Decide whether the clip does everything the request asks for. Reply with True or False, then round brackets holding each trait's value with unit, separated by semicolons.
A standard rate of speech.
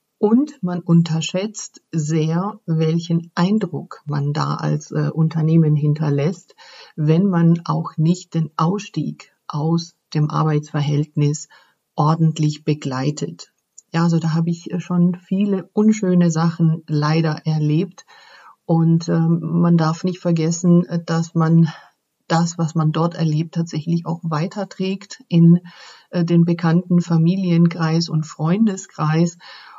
False (115 wpm)